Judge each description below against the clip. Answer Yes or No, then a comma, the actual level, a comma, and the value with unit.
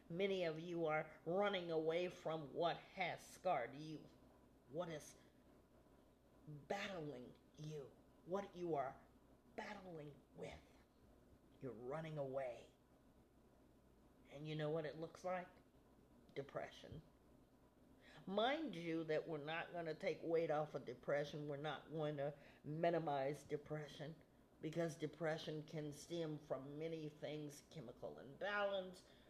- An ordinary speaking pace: No, slow, 120 wpm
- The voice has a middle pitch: Yes, medium, 155 Hz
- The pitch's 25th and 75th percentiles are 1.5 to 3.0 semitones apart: Yes, narrow, 2.4 semitones